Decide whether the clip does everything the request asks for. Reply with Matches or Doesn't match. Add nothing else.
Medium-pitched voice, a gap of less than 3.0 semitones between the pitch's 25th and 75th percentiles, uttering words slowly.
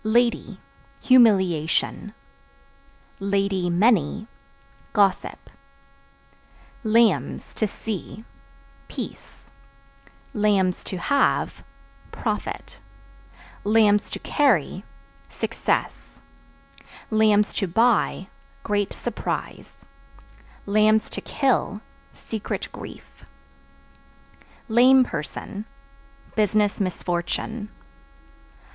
Doesn't match